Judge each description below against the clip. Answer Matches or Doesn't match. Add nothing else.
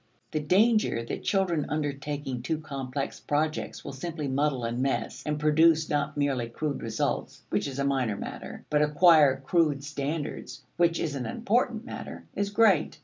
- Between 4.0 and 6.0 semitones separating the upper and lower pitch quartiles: Doesn't match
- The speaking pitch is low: Doesn't match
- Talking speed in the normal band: Matches